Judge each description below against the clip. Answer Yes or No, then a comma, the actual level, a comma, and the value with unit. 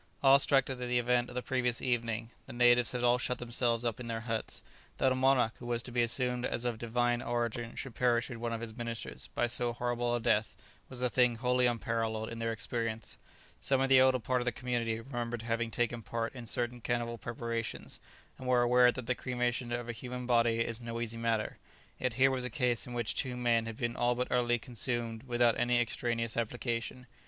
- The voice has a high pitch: No, low, 120 Hz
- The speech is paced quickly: Yes, fast, 220 wpm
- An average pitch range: No, narrow, 1.2 semitones